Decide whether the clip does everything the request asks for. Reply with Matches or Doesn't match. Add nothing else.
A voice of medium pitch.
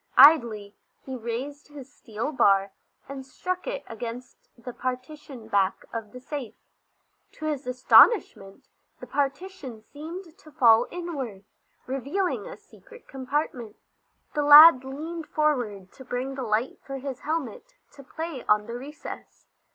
Doesn't match